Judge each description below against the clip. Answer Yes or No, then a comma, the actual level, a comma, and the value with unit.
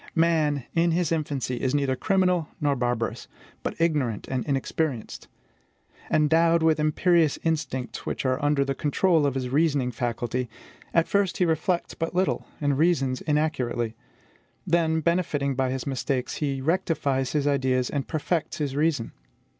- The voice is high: No, medium, 145 Hz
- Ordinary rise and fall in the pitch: Yes, average, 3.8 semitones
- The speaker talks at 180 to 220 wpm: No, average, 145 wpm